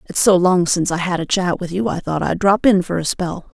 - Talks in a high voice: No, medium, 180 Hz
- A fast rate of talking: Yes, fast, 300 wpm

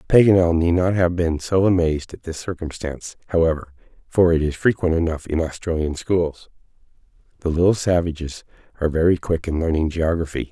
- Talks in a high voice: No, very low, 85 Hz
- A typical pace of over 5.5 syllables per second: Yes, 5.7 syllables/s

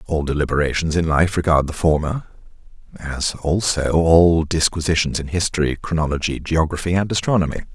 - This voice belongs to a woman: No, male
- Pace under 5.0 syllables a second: No, 5.5 syllables/s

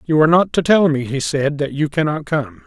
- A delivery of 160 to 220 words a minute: No, fast, 270 wpm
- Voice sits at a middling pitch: Yes, medium, 150 Hz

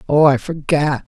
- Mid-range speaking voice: Yes, medium, 150 Hz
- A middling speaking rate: Yes, average, 150 wpm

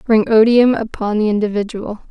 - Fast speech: No, average, 145 wpm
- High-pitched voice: Yes, high, 220 Hz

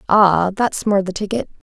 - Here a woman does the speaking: Yes, female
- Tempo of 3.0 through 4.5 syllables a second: Yes, 4.4 syllables/s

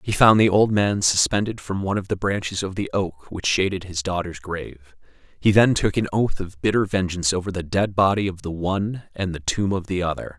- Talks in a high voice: No, very low, 95 Hz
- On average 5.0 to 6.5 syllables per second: Yes, 5.5 syllables/s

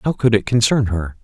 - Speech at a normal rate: No, fast, 240 wpm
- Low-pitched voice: Yes, low, 110 Hz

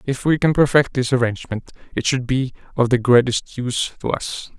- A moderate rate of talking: Yes, average, 195 wpm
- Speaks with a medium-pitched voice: No, low, 125 Hz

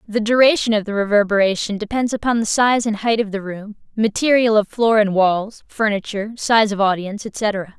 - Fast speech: No, average, 185 wpm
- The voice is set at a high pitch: Yes, high, 215 Hz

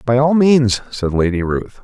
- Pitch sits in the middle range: No, low, 120 Hz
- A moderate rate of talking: Yes, average, 195 wpm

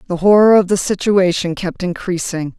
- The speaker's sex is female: Yes, female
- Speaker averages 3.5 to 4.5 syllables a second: No, 5.0 syllables/s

